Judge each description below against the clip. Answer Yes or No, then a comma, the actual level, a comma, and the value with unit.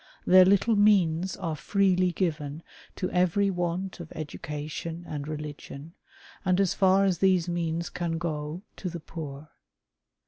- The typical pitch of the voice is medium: Yes, medium, 175 Hz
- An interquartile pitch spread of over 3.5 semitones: No, average, 3.0 semitones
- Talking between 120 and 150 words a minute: Yes, average, 140 wpm